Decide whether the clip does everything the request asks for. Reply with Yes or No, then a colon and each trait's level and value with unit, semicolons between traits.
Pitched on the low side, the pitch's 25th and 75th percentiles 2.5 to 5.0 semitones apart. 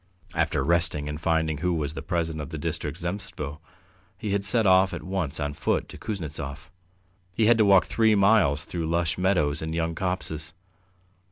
Yes: very low, 85 Hz; average, 3.9 semitones